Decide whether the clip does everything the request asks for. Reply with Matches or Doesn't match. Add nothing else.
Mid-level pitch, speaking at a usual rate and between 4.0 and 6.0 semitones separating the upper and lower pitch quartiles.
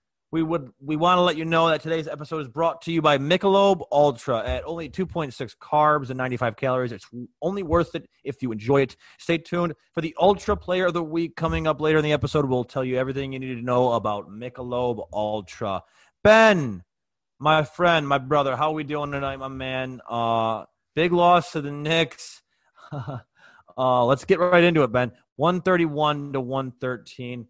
Matches